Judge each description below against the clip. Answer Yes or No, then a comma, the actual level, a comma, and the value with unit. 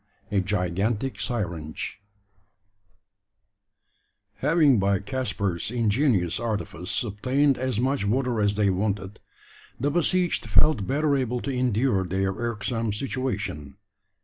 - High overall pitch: No, low, 110 Hz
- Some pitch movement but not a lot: Yes, average, 5.0 semitones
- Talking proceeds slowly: Yes, slow, 105 wpm